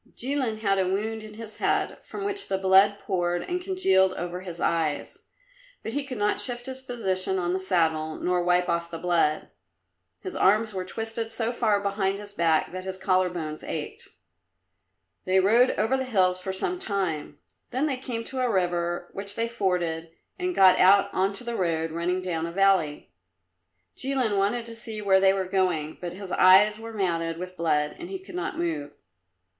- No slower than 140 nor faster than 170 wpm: No, average, 190 wpm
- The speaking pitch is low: No, high, 190 Hz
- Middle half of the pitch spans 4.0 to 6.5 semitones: Yes, average, 4.3 semitones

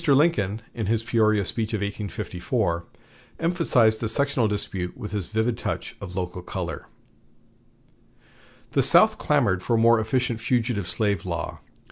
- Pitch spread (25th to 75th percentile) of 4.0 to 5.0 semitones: No, average, 3.1 semitones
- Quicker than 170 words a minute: No, average, 140 wpm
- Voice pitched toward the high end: No, low, 110 Hz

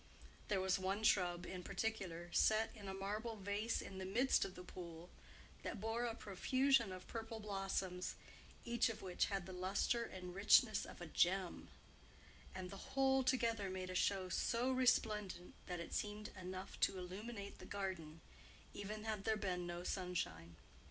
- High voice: Yes, high, 195 Hz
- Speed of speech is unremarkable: Yes, average, 165 wpm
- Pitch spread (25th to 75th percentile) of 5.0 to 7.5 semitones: No, average, 3.4 semitones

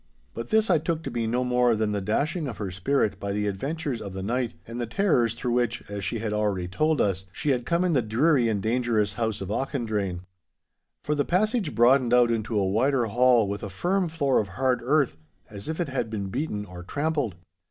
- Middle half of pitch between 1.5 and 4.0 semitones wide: No, average, 5.3 semitones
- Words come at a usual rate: No, fast, 225 wpm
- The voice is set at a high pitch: No, low, 120 Hz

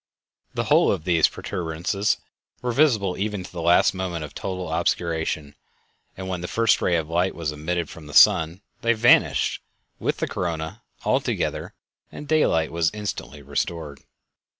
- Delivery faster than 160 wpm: No, average, 155 wpm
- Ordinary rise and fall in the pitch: Yes, average, 3.4 semitones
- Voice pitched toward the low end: Yes, very low, 85 Hz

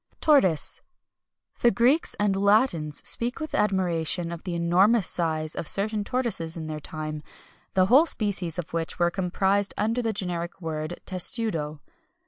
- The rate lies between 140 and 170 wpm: Yes, average, 145 wpm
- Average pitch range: Yes, average, 4.6 semitones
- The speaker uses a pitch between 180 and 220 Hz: Yes, medium, 185 Hz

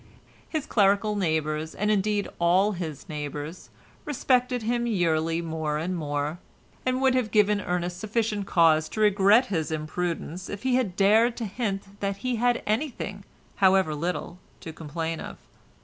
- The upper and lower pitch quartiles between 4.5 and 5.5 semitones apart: Yes, average, 4.9 semitones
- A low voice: No, high, 195 Hz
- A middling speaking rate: Yes, average, 150 wpm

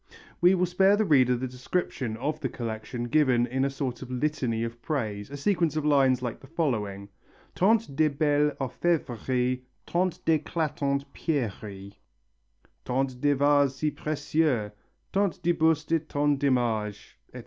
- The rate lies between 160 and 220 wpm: No, average, 150 wpm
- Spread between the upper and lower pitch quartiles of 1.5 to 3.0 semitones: No, average, 4.1 semitones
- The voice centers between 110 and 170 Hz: Yes, medium, 140 Hz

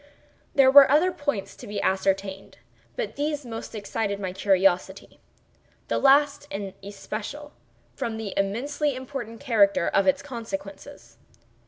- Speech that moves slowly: Yes, slow, 125 wpm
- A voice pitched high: Yes, high, 225 Hz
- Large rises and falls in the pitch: Yes, wide, 6.3 semitones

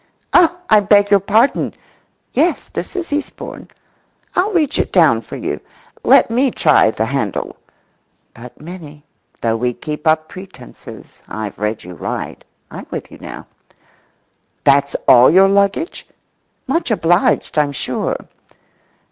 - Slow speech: Yes, slow, 125 wpm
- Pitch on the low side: No, medium, 175 Hz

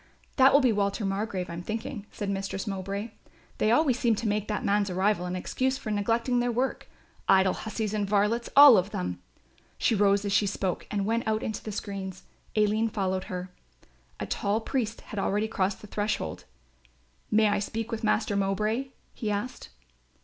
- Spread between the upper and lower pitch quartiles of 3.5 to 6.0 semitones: No, narrow, 2.4 semitones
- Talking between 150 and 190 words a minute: Yes, average, 180 wpm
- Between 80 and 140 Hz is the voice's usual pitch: No, high, 210 Hz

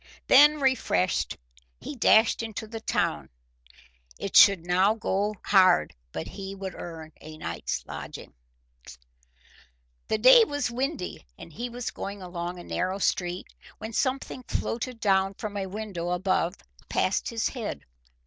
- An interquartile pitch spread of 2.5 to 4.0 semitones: No, average, 4.4 semitones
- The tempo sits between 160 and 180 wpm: No, average, 140 wpm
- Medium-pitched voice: No, high, 200 Hz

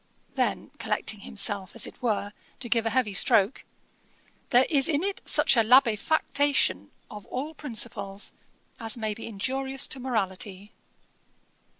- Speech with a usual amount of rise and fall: Yes, average, 4.6 semitones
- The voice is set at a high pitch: Yes, high, 230 Hz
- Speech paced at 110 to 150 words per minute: Yes, slow, 135 wpm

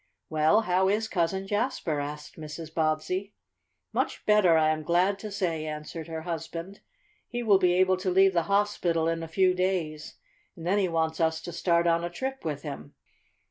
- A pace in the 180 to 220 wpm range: Yes, average, 185 wpm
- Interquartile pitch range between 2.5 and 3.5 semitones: Yes, average, 3.1 semitones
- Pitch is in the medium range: Yes, medium, 170 Hz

